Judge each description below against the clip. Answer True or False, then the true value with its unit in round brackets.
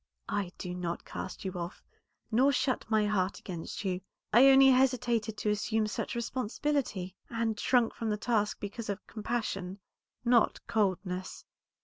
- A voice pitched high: True (215 Hz)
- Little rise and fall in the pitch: False (3.8 semitones)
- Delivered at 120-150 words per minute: True (145 wpm)